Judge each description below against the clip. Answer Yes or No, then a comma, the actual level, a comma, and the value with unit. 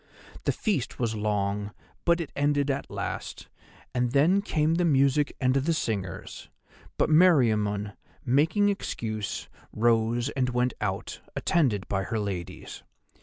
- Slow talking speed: Yes, slow, 130 wpm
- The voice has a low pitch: Yes, low, 125 Hz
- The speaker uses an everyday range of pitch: No, wide, 6.0 semitones